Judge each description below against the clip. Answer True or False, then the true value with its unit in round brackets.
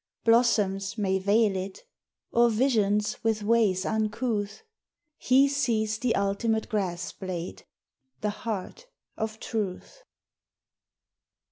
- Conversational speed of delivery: False (100 wpm)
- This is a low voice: False (215 Hz)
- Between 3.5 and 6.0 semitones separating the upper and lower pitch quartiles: False (2.7 semitones)